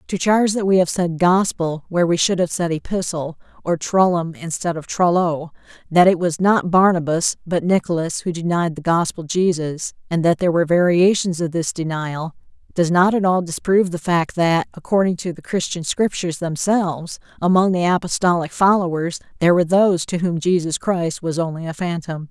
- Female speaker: Yes, female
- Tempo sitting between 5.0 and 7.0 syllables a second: Yes, 5.3 syllables/s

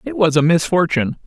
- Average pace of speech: Yes, average, 190 wpm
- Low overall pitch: No, medium, 165 Hz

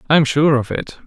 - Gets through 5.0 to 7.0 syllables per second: Yes, 6.2 syllables/s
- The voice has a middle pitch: Yes, medium, 145 Hz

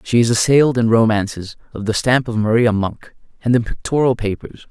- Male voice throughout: Yes, male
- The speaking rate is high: No, average, 190 wpm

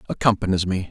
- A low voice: Yes, very low, 95 Hz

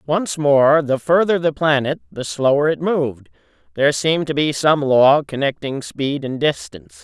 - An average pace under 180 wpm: Yes, average, 170 wpm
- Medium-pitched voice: Yes, medium, 145 Hz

